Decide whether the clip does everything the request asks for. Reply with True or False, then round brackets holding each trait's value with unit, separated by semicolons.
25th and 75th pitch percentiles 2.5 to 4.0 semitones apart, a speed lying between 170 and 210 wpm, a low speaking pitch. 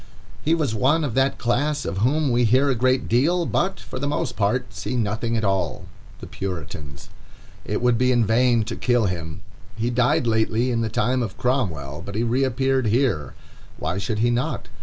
True (3.7 semitones; 190 wpm; 120 Hz)